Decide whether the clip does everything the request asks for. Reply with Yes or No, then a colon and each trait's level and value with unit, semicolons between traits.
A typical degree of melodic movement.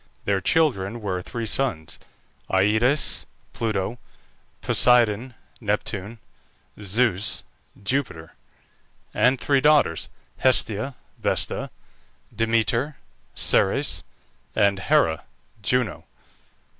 Yes: average, 4.2 semitones